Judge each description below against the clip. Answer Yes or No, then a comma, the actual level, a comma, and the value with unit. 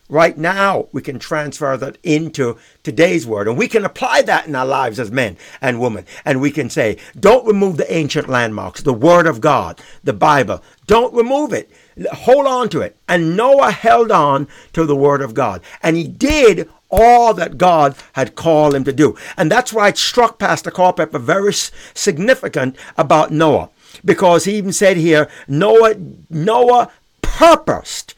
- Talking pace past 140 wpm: Yes, average, 175 wpm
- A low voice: No, medium, 165 Hz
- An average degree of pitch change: No, wide, 6.7 semitones